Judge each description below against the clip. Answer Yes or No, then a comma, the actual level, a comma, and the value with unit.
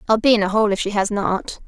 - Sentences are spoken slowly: No, fast, 320 wpm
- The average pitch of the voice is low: No, high, 210 Hz